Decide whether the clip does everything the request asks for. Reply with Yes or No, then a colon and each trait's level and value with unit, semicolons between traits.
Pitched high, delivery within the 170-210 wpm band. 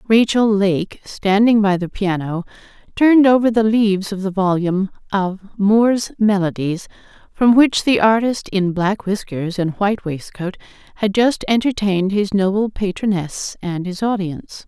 No: high, 200 Hz; average, 145 wpm